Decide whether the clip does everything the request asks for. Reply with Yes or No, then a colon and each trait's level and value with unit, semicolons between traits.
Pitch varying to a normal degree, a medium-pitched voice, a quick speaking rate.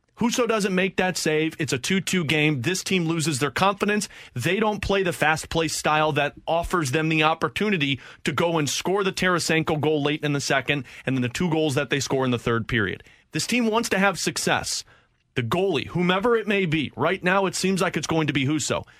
Yes: average, 4.2 semitones; medium, 165 Hz; fast, 225 wpm